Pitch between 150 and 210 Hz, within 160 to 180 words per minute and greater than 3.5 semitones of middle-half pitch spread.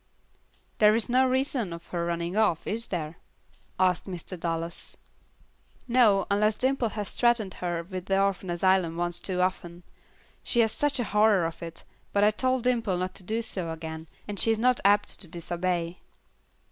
Yes: high, 190 Hz; average, 175 wpm; average, 4.3 semitones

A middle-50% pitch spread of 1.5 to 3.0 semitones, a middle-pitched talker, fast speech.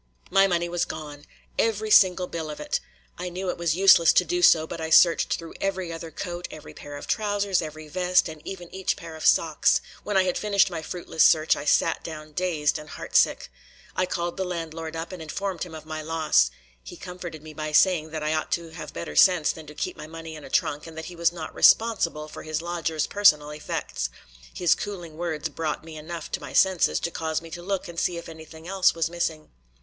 Yes: narrow, 2.4 semitones; medium, 165 Hz; fast, 225 wpm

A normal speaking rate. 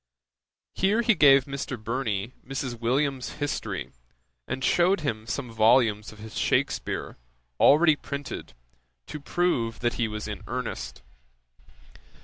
No: slow, 125 wpm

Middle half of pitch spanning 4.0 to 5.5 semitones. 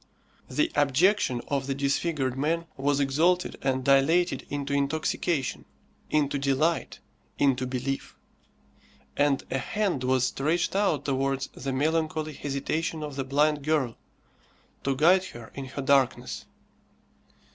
No: average, 2.8 semitones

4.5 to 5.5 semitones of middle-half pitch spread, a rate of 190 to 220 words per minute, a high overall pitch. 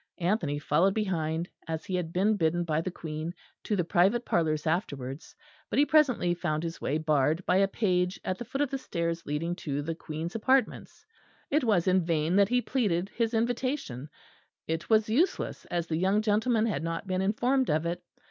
No: average, 5.1 semitones; average, 195 wpm; medium, 180 Hz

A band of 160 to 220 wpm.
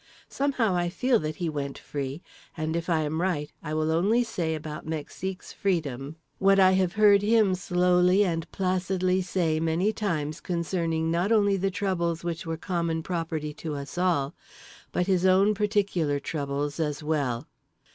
Yes: average, 165 wpm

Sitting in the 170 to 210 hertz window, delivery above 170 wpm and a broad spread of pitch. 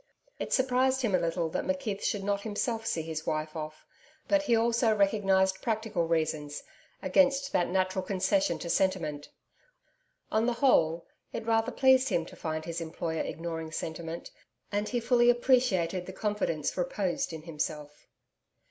No: high, 190 Hz; average, 155 wpm; wide, 6.1 semitones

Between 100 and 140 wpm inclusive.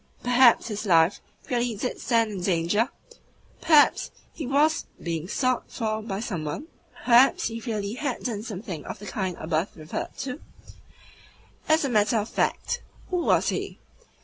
No: average, 160 wpm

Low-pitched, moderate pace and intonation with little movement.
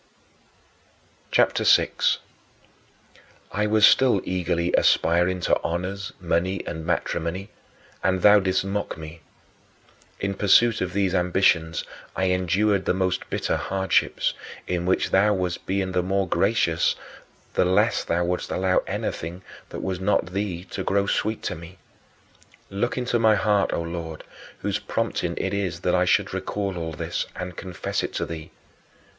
Yes: very low, 95 Hz; average, 150 wpm; narrow, 2.2 semitones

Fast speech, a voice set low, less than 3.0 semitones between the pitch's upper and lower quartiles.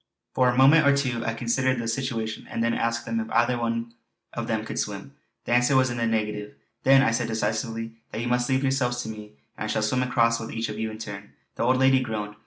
Yes: fast, 240 wpm; low, 115 Hz; narrow, 2.4 semitones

